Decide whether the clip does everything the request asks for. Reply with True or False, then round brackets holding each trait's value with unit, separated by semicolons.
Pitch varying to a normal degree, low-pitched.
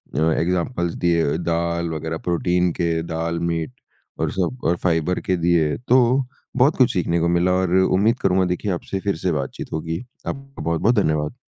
False (2.1 semitones; 85 Hz)